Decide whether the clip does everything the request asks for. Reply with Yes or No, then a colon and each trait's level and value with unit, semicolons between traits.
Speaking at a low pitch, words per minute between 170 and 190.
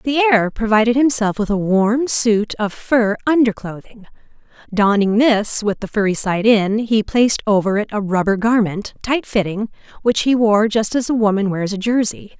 No: high, 215 Hz; average, 185 wpm